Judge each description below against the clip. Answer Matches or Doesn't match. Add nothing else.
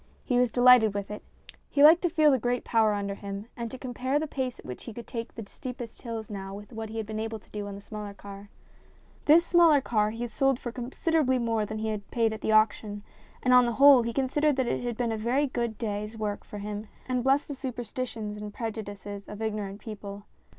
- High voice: Matches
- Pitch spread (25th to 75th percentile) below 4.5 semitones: Matches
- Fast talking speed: Matches